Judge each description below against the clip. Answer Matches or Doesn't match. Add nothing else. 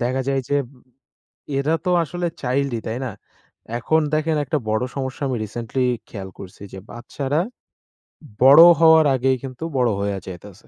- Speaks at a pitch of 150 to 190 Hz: Doesn't match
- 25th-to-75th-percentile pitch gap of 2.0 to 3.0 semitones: Doesn't match